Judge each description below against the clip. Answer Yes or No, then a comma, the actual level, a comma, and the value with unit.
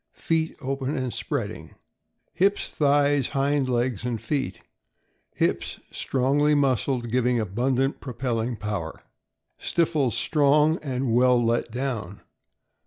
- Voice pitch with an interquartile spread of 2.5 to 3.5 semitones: Yes, average, 3.2 semitones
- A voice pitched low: Yes, low, 130 Hz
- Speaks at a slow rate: Yes, slow, 115 wpm